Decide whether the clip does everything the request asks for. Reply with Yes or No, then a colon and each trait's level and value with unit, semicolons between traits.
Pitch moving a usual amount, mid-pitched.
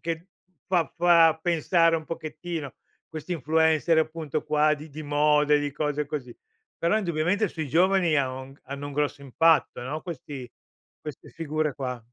No: narrow, 2.3 semitones; medium, 155 Hz